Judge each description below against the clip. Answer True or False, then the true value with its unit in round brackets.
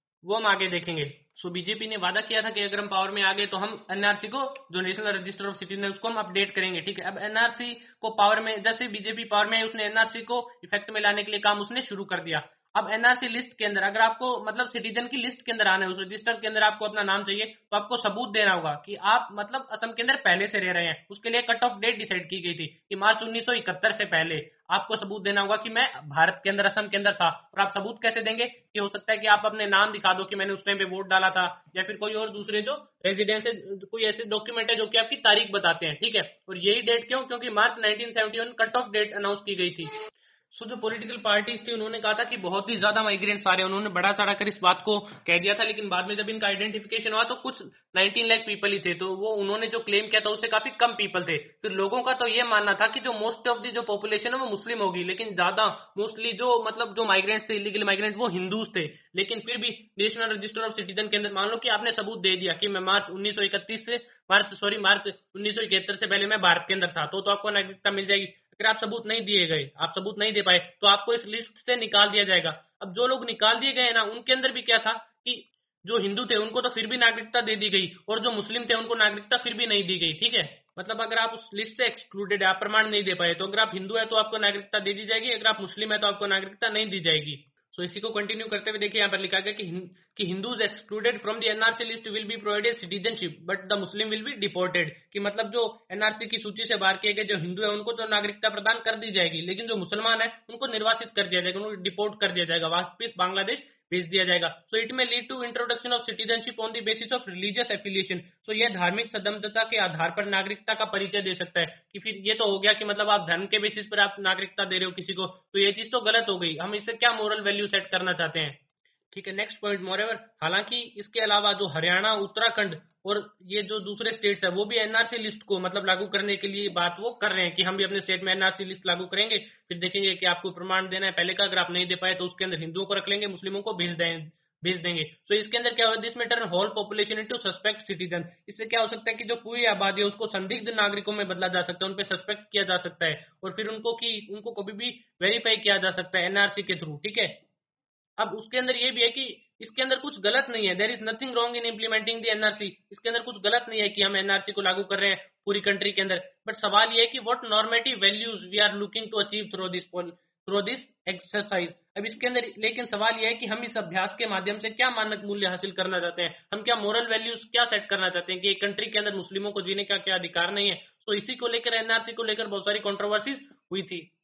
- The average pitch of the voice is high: True (210 Hz)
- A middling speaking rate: False (260 wpm)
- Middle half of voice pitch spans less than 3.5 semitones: True (2.7 semitones)